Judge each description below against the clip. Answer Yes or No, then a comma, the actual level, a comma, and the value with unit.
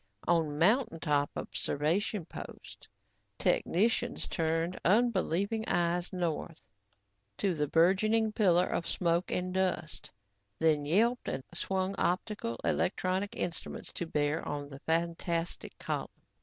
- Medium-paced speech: No, slow, 115 wpm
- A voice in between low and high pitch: Yes, medium, 175 Hz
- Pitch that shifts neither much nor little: Yes, average, 3.3 semitones